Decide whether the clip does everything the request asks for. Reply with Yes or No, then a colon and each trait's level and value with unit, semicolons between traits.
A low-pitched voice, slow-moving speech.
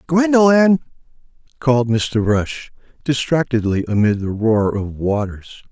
Yes: low, 125 Hz; slow, 105 wpm